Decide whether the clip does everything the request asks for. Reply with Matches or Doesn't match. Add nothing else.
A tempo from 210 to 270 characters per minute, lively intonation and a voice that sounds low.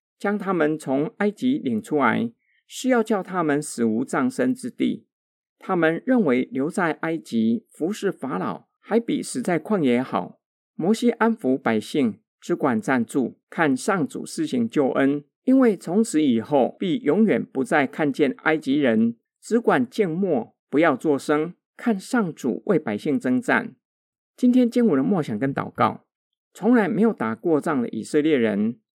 Doesn't match